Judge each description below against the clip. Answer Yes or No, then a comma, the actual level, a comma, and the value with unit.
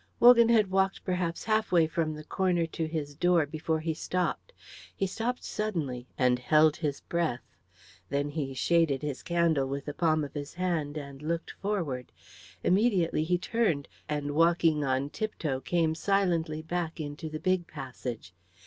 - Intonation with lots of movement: No, average, 3.6 semitones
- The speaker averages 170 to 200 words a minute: No, average, 160 wpm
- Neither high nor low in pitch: Yes, medium, 160 Hz